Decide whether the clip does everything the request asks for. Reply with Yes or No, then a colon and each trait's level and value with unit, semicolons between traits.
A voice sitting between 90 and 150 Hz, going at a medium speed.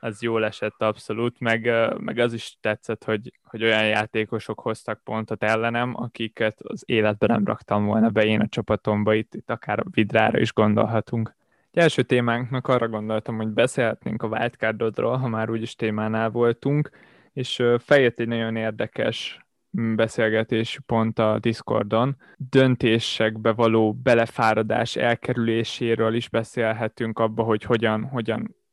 Yes: low, 115 Hz; average, 140 wpm